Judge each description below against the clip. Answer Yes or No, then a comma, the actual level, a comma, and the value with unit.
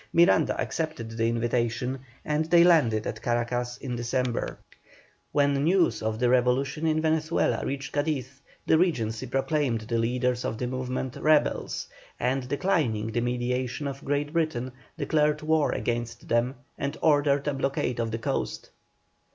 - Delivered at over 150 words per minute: No, average, 145 wpm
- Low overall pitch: Yes, low, 130 Hz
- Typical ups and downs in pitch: Yes, average, 4.0 semitones